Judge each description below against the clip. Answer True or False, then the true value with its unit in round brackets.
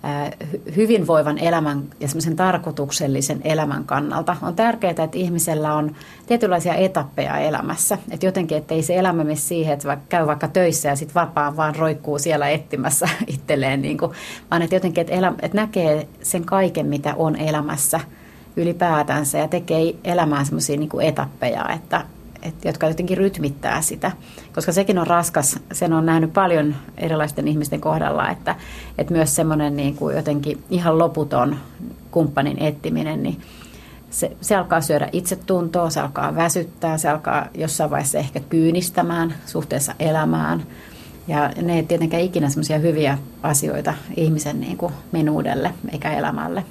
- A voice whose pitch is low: False (160 Hz)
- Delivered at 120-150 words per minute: True (145 wpm)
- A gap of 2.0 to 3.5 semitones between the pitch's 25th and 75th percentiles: True (2.7 semitones)